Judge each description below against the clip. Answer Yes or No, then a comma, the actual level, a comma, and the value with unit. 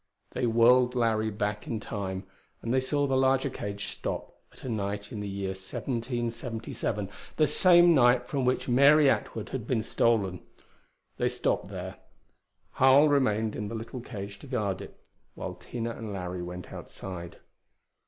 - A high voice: No, low, 115 Hz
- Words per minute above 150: Yes, average, 160 wpm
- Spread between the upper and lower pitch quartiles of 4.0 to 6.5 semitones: Yes, average, 4.3 semitones